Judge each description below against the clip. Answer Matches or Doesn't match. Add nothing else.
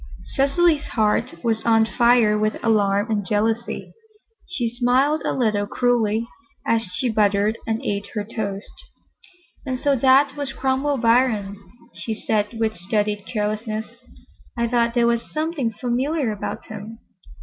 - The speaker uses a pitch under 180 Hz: Doesn't match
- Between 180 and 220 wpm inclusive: Doesn't match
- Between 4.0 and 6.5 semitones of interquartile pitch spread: Doesn't match